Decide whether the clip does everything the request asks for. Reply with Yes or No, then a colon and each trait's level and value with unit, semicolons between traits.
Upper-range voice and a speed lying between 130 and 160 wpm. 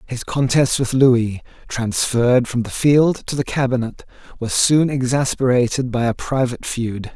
No: low, 125 Hz; average, 150 wpm